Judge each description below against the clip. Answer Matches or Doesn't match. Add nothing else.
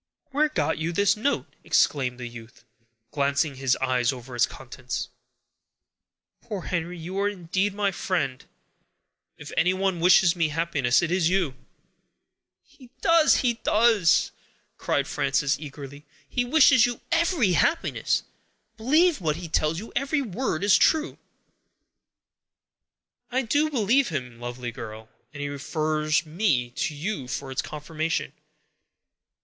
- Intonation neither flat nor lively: Doesn't match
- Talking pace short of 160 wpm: Matches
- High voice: Doesn't match